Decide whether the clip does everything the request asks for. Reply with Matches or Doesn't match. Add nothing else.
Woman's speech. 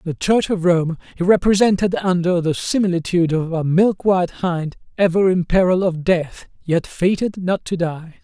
Doesn't match